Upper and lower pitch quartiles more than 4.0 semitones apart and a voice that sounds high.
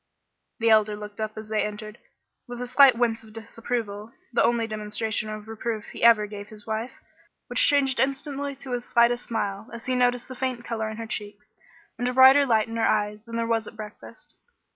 No: narrow, 2.4 semitones; high, 225 Hz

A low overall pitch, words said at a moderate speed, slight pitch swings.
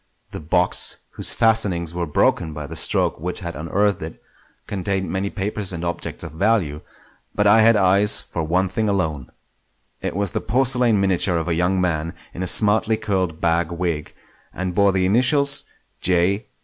No: very low, 95 Hz; average, 175 wpm; average, 3.4 semitones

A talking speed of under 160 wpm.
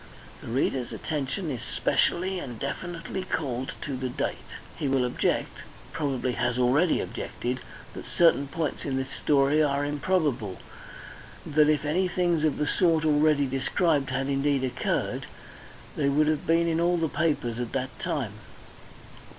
Yes: average, 150 wpm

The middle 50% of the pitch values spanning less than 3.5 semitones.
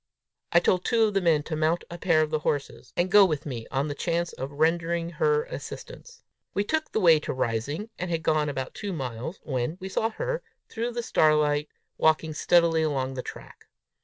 No: average, 4.4 semitones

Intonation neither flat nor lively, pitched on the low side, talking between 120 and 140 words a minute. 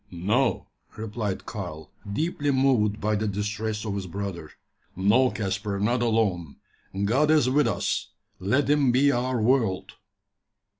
Yes: average, 4.3 semitones; low, 110 Hz; slow, 135 wpm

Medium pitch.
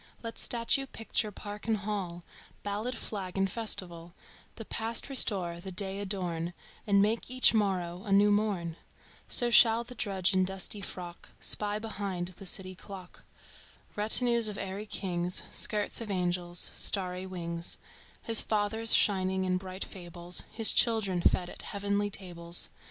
No: high, 195 Hz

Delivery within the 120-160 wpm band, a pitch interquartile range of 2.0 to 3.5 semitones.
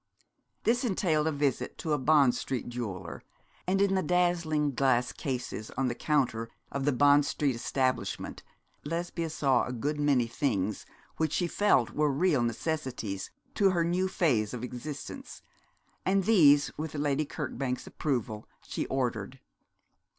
No: average, 145 wpm; average, 4.4 semitones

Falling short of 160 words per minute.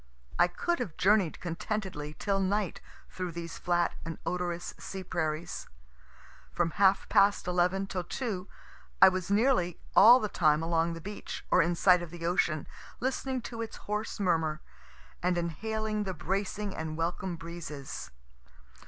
Yes: average, 150 wpm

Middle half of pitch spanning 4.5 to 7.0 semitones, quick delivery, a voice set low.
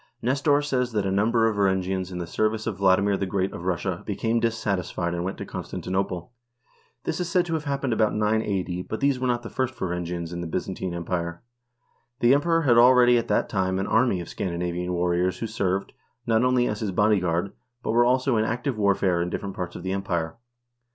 Yes: average, 4.9 semitones; fast, 210 wpm; low, 100 Hz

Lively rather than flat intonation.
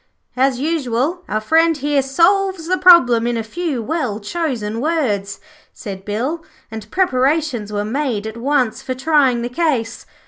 Yes: wide, 6.1 semitones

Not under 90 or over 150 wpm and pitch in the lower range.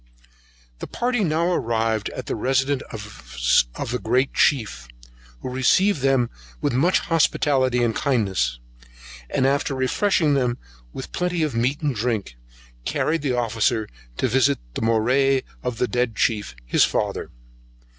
Yes: average, 140 wpm; low, 125 Hz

